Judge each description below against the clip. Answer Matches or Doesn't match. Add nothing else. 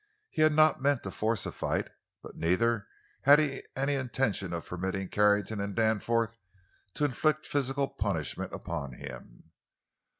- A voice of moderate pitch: Doesn't match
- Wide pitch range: Matches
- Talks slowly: Doesn't match